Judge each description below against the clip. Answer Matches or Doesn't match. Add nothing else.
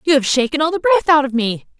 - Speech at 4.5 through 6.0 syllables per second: Doesn't match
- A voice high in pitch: Matches